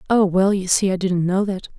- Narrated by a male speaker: No, female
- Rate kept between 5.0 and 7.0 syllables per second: Yes, 5.2 syllables/s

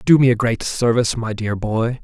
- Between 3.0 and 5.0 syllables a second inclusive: No, 5.2 syllables/s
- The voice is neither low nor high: No, low, 115 Hz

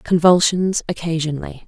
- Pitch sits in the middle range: Yes, medium, 170 Hz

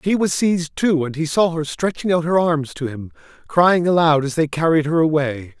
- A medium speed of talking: No, fast, 225 wpm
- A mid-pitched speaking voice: Yes, medium, 160 Hz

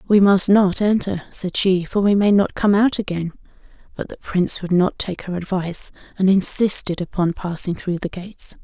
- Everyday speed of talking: Yes, average, 195 wpm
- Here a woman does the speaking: Yes, female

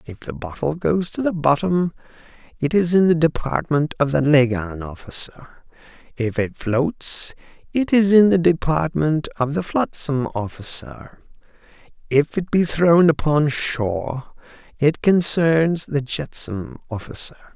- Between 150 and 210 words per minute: No, slow, 135 wpm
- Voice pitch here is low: No, medium, 145 Hz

